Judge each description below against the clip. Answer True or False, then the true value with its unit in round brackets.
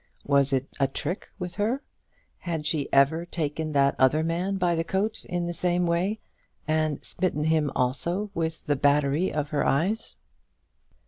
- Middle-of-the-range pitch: True (160 Hz)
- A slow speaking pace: False (160 wpm)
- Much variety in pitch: False (3.6 semitones)